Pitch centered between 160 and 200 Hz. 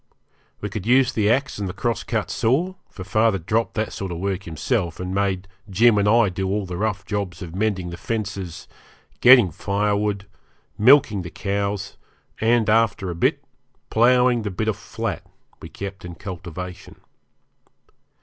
No: low, 100 Hz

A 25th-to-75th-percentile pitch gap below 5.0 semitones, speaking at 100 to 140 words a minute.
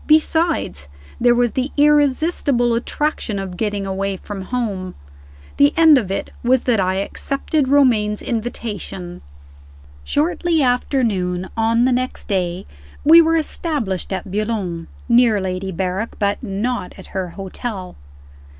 No: average, 5.3 semitones; slow, 135 wpm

